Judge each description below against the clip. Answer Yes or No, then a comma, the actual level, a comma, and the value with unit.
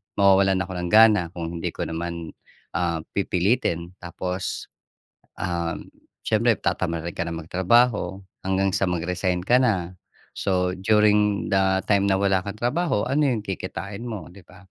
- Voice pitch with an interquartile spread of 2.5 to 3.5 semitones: Yes, average, 2.8 semitones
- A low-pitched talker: Yes, very low, 95 Hz